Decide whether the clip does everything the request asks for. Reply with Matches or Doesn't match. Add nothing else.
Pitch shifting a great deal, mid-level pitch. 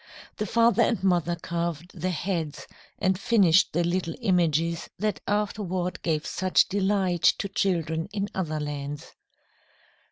Doesn't match